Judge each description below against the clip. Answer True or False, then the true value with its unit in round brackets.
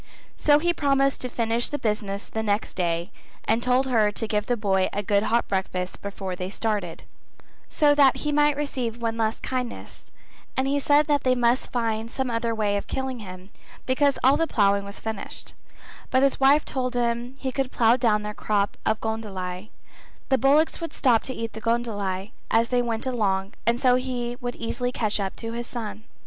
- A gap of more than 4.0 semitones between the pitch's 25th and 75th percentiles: False (3.7 semitones)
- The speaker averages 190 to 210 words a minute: True (195 wpm)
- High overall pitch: True (230 Hz)